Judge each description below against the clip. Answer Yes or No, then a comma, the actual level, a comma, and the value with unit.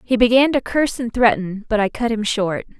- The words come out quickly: Yes, fast, 235 wpm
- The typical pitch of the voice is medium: No, high, 230 Hz